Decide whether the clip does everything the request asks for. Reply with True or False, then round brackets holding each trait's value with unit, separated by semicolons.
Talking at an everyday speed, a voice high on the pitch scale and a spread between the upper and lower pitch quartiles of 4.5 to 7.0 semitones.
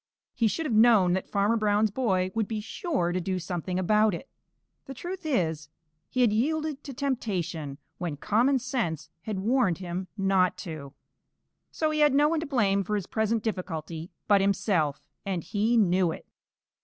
True (175 wpm; 205 Hz; 5.2 semitones)